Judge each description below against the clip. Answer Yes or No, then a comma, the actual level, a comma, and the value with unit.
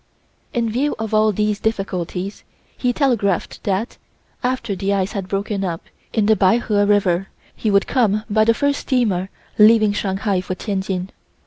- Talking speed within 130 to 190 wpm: Yes, average, 155 wpm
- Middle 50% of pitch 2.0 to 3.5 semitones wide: Yes, narrow, 2.6 semitones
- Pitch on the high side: Yes, high, 205 Hz